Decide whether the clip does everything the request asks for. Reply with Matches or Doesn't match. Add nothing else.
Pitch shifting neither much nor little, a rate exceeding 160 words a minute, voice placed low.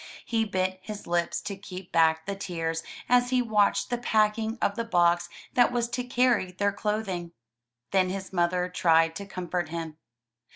Doesn't match